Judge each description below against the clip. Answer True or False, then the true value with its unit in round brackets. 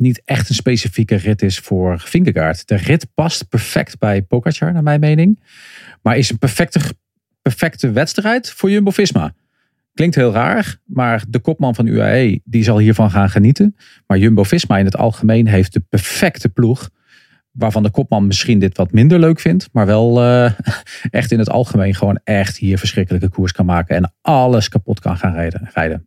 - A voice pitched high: False (115 Hz)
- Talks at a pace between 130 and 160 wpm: False (175 wpm)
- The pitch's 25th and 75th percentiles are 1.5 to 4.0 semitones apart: False (5.4 semitones)